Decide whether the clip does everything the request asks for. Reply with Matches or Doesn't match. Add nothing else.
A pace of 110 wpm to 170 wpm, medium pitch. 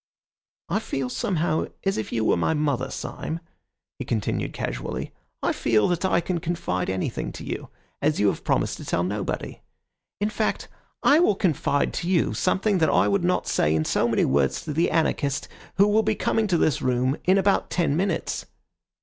Doesn't match